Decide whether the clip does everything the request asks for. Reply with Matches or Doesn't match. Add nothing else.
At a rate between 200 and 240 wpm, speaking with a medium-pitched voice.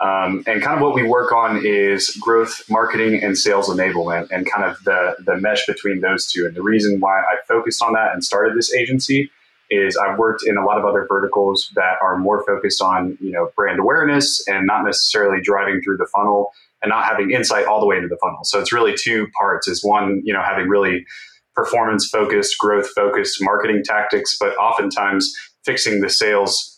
Doesn't match